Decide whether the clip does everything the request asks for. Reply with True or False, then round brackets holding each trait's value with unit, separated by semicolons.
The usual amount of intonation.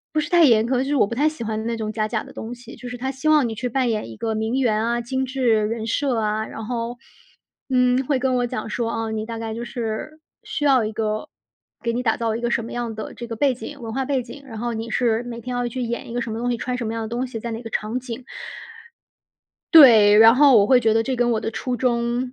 False (2.2 semitones)